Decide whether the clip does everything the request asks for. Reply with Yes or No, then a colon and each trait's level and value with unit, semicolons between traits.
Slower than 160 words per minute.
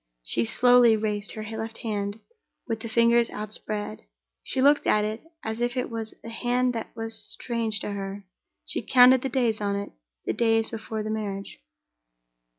No: average, 170 wpm